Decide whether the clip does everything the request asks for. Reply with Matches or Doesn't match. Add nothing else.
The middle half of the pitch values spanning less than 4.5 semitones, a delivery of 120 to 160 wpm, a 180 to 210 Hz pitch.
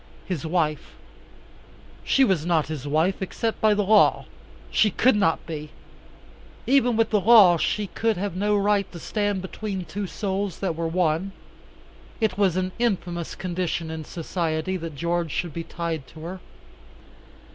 Matches